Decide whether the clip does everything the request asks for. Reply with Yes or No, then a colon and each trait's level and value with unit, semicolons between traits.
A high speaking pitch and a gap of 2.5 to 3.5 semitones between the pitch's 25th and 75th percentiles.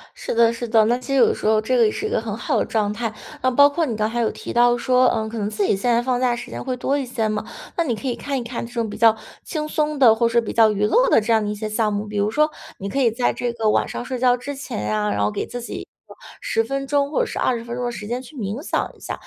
Yes: high, 235 Hz; average, 3.0 semitones